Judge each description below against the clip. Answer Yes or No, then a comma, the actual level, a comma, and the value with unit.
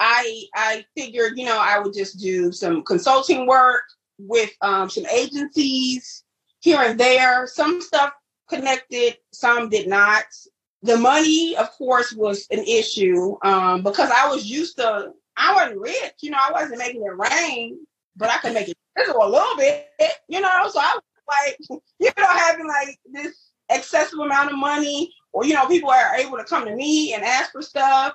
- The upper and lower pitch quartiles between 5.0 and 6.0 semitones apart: Yes, average, 5.3 semitones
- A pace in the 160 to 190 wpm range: Yes, average, 180 wpm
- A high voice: Yes, very high, 270 Hz